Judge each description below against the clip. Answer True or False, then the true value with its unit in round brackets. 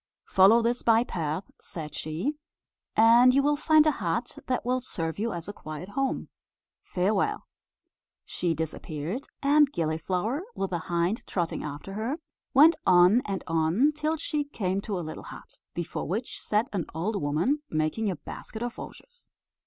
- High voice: True (205 Hz)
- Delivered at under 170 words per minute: True (160 wpm)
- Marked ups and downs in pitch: True (7.2 semitones)